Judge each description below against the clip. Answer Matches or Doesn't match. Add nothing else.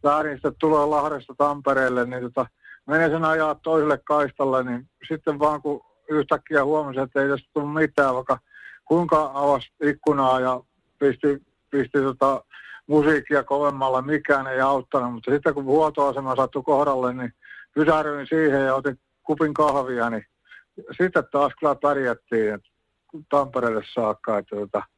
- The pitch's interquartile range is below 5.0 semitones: Matches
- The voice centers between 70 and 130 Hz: Doesn't match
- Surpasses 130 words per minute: Matches